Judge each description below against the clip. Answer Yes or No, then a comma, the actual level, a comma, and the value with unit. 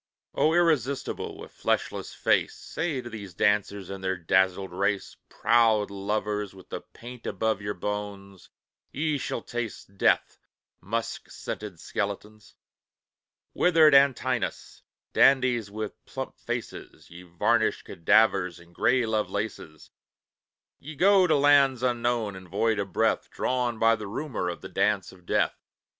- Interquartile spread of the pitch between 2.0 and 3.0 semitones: No, average, 4.2 semitones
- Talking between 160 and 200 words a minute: No, slow, 135 wpm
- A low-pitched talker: Yes, low, 110 Hz